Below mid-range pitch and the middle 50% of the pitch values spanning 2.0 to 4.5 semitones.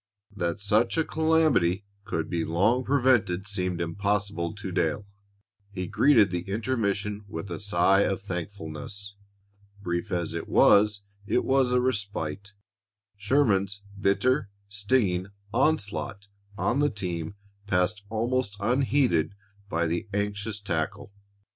Yes: low, 100 Hz; average, 3.7 semitones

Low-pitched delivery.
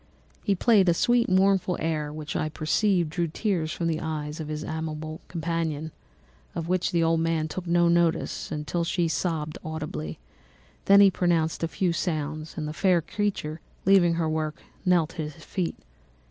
No: medium, 165 Hz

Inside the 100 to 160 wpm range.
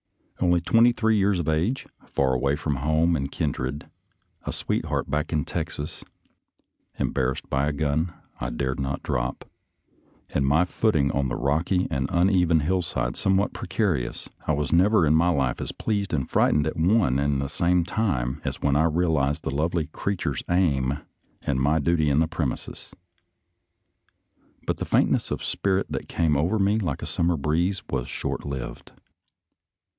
No: average, 170 wpm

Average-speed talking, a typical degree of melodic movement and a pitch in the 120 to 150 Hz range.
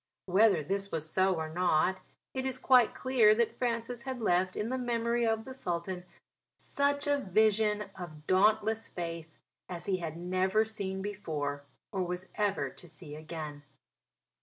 No: average, 160 wpm; average, 4.4 semitones; high, 190 Hz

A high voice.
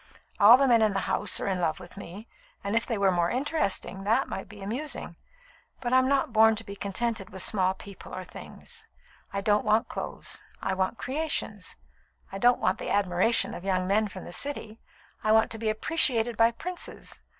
Yes: high, 215 Hz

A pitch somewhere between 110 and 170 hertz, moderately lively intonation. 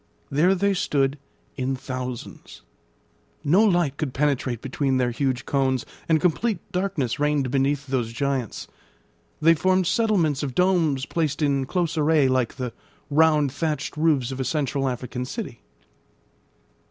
Yes: medium, 140 Hz; average, 3.7 semitones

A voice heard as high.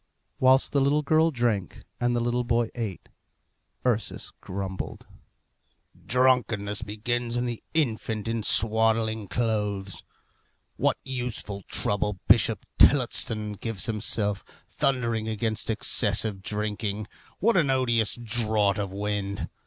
No: low, 110 Hz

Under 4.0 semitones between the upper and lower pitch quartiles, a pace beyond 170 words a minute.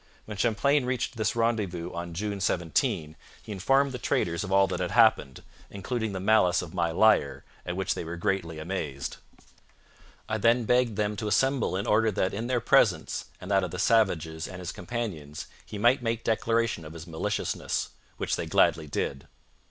No: average, 4.9 semitones; average, 185 wpm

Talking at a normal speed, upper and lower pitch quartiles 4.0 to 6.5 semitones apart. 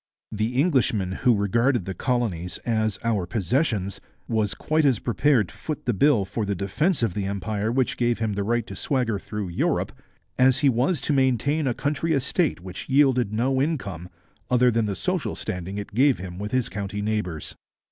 Yes: average, 190 wpm; average, 4.7 semitones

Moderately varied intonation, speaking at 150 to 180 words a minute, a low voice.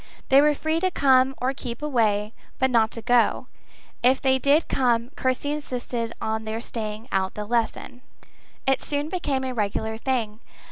No: average, 3.4 semitones; average, 170 wpm; very high, 250 Hz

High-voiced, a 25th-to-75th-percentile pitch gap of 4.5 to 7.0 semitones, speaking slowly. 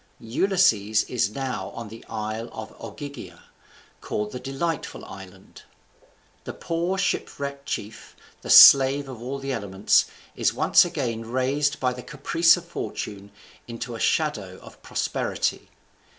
No: low, 125 Hz; average, 4.9 semitones; slow, 130 wpm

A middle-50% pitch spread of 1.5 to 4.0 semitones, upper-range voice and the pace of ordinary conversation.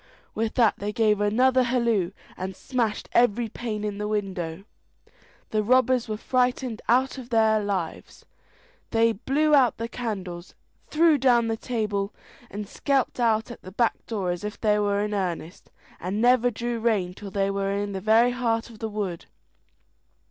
Yes: average, 3.1 semitones; high, 220 Hz; average, 170 wpm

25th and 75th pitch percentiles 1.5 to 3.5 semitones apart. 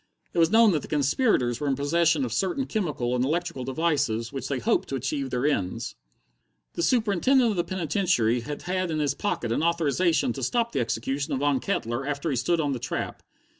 No: average, 4.9 semitones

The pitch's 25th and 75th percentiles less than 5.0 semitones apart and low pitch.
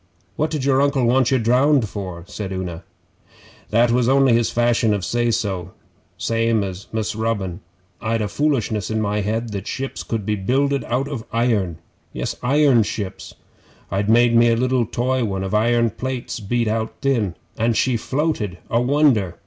Yes: average, 3.6 semitones; low, 115 Hz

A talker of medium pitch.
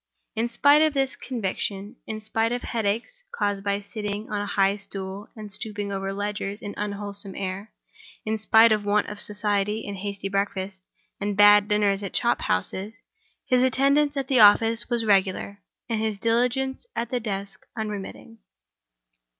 No: high, 210 Hz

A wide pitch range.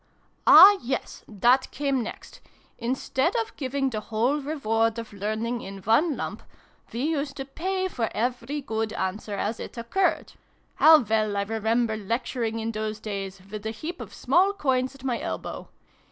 No: average, 3.9 semitones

